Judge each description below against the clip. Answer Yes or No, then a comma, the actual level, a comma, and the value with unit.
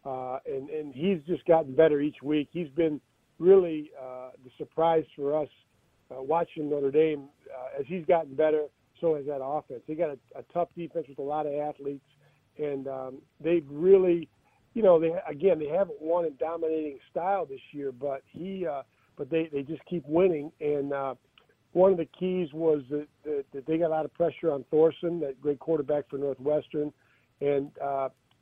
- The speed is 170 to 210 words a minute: Yes, average, 190 wpm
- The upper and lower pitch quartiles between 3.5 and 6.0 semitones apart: No, average, 3.1 semitones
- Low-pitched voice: No, medium, 150 Hz